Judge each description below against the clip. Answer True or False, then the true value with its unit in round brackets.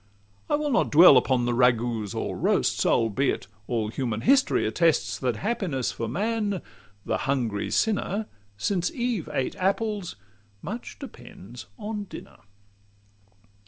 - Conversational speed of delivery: False (125 wpm)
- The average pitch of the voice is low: False (150 Hz)